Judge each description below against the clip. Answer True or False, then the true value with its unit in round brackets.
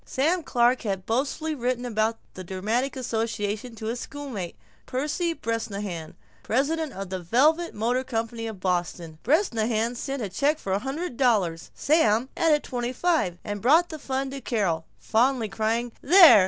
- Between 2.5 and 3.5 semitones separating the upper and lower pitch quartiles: False (4.8 semitones)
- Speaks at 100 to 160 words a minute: True (155 wpm)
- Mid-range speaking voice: False (235 Hz)